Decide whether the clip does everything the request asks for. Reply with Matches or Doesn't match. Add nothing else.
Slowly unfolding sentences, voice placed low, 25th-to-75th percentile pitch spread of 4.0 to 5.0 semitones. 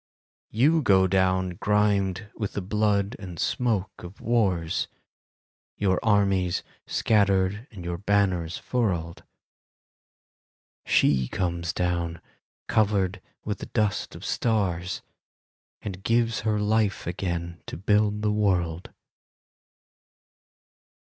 Doesn't match